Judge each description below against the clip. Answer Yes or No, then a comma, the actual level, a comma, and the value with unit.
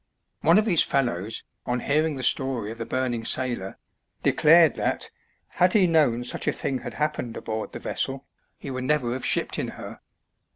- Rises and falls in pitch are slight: No, average, 4.2 semitones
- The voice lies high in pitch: No, low, 130 Hz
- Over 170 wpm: Yes, average, 180 wpm